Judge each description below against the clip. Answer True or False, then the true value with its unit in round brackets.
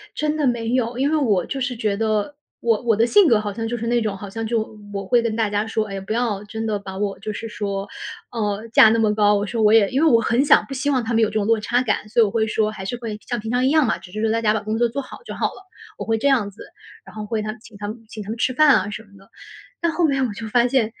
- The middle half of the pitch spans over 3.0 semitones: False (2.4 semitones)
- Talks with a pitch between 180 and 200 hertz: False (225 Hz)